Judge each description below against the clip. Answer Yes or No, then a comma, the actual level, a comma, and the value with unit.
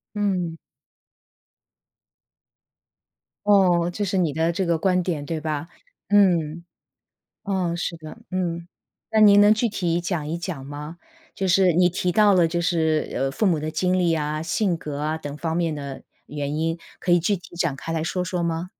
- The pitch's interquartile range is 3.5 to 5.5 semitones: No, average, 2.7 semitones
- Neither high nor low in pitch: Yes, medium, 170 Hz